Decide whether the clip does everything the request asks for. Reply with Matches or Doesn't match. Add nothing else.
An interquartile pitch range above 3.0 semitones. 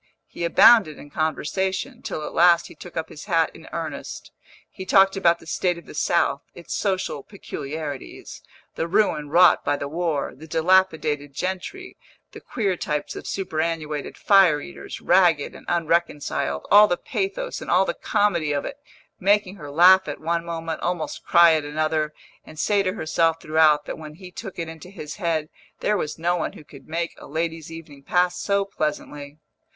Matches